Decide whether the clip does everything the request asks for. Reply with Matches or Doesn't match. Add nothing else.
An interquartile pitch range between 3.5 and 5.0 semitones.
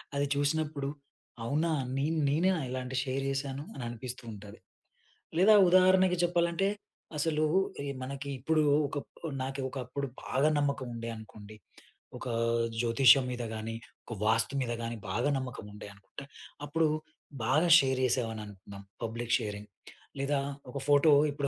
Matches